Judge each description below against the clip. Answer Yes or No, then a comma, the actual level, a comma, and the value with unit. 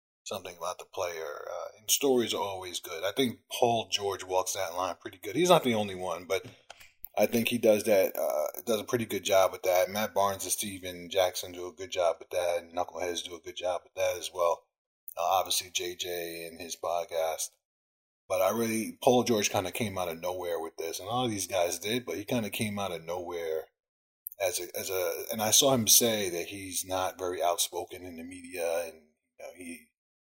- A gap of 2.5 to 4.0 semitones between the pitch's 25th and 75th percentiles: No, wide, 5.6 semitones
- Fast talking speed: Yes, fast, 220 wpm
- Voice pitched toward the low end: Yes, low, 100 Hz